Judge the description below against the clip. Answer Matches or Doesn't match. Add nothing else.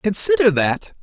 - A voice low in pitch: Doesn't match